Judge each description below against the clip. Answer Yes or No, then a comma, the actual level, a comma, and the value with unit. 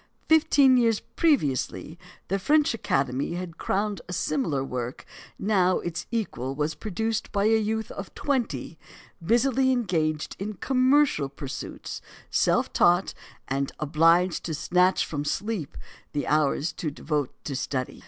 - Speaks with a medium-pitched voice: Yes, medium, 180 Hz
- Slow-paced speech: Yes, slow, 130 wpm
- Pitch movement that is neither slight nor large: No, wide, 7.1 semitones